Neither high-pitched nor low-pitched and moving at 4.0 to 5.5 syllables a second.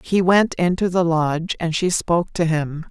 Yes: medium, 170 Hz; 4.7 syllables/s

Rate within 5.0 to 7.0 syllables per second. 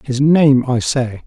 No: 3.5 syllables/s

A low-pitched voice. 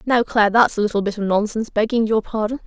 No: high, 215 Hz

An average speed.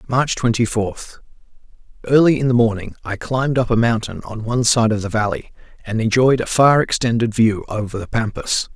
Yes: average, 180 wpm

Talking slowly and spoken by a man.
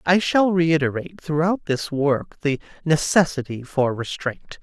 Yes: slow, 130 wpm; male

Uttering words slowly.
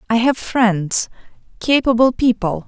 Yes: slow, 110 wpm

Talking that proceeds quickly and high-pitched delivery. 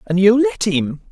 Yes: fast, 215 wpm; high, 205 Hz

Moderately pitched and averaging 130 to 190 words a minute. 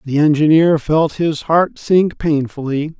Yes: medium, 155 Hz; average, 140 wpm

